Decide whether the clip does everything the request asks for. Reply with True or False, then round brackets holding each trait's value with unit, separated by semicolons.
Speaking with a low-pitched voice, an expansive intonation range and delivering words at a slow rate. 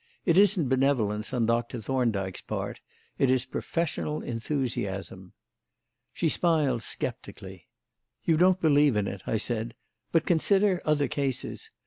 True (130 Hz; 5.8 semitones; 125 wpm)